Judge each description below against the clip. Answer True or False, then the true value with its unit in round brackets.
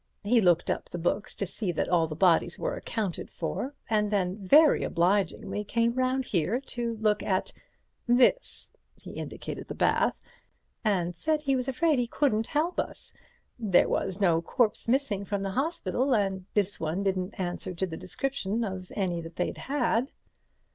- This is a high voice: True (210 Hz)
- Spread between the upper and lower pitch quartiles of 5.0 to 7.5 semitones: True (5.4 semitones)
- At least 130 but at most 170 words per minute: True (160 wpm)